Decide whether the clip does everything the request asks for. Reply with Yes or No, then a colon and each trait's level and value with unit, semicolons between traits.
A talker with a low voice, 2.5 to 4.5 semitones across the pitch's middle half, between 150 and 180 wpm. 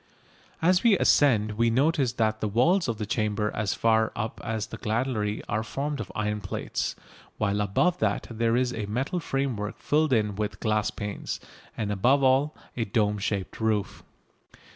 Yes: low, 110 Hz; average, 3.9 semitones; average, 170 wpm